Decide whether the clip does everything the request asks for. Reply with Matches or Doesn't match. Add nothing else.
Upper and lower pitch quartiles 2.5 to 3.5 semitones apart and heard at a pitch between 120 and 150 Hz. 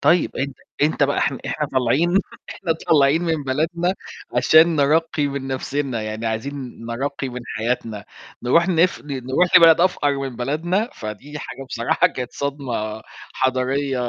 Doesn't match